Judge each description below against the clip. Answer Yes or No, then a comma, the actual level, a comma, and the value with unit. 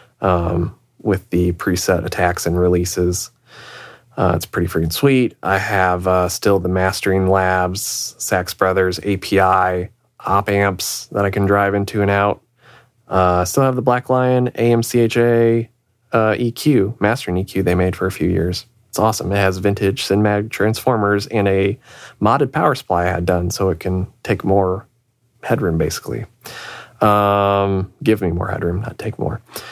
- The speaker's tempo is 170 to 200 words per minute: No, average, 160 wpm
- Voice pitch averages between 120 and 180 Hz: No, low, 100 Hz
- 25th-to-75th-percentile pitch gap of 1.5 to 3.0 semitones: No, average, 3.7 semitones